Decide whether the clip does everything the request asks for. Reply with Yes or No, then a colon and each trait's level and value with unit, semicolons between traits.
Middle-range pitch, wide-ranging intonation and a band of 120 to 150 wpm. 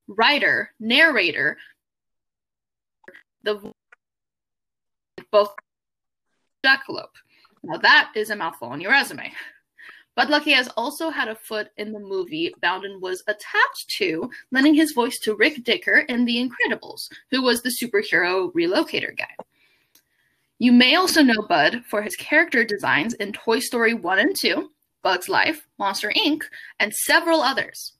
No: very high, 255 Hz; wide, 6.8 semitones; slow, 135 wpm